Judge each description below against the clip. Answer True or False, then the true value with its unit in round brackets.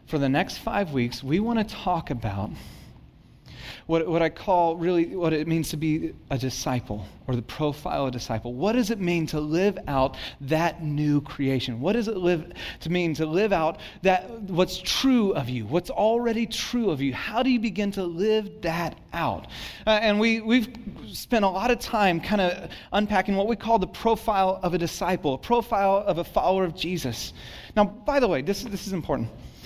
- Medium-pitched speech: True (180 Hz)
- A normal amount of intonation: False (5.7 semitones)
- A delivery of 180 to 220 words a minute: True (200 wpm)